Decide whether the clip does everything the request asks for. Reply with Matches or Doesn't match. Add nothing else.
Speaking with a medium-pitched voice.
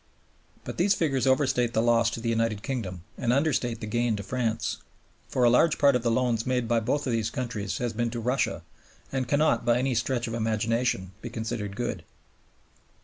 Doesn't match